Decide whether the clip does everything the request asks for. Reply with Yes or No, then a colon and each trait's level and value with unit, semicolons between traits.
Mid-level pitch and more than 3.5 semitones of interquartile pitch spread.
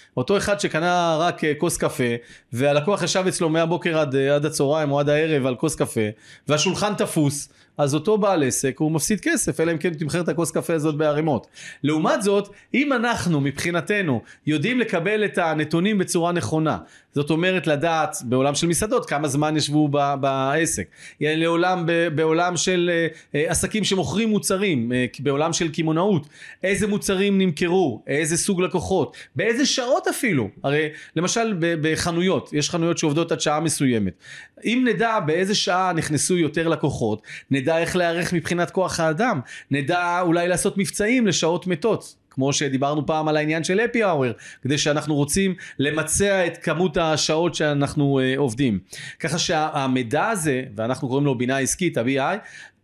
Yes: medium, 165 Hz; average, 4.0 semitones